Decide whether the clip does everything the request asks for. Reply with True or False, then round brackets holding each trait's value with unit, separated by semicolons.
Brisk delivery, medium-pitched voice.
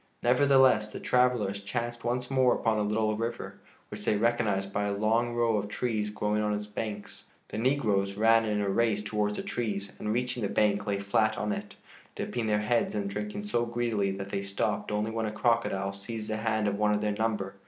False (210 wpm; 110 Hz)